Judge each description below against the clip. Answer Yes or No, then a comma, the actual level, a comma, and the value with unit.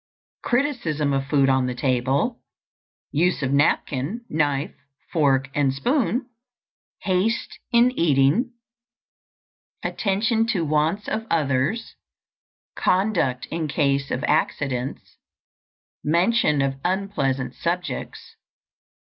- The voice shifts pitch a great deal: Yes, wide, 7.1 semitones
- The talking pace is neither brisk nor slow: No, slow, 95 wpm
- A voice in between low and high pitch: Yes, medium, 155 Hz